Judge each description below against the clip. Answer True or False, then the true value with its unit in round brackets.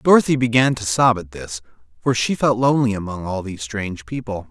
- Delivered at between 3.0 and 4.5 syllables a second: False (6.0 syllables/s)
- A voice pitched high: False (110 Hz)